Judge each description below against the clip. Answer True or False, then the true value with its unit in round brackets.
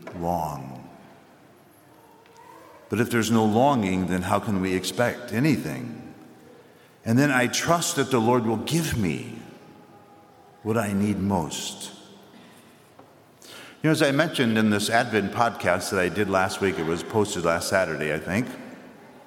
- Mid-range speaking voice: False (105 Hz)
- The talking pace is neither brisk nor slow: True (145 wpm)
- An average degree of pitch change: True (4.3 semitones)